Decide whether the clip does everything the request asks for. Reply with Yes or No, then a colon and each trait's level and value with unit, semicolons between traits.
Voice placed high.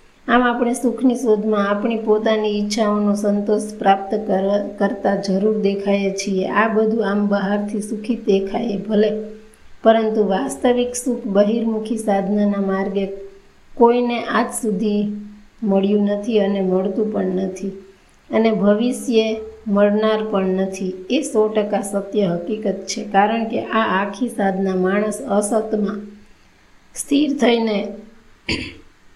Yes: high, 210 Hz